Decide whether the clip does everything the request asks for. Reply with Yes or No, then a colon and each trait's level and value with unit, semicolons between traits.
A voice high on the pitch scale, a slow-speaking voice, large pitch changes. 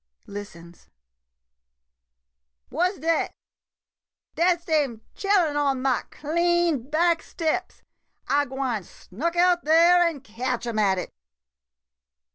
Yes: very high, 300 Hz; slow, 110 wpm; wide, 5.9 semitones